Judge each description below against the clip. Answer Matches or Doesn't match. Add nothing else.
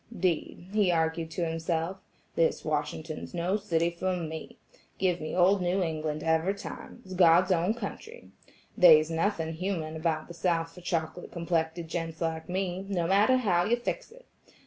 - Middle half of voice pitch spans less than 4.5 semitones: Matches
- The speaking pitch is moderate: Matches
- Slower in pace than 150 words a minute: Doesn't match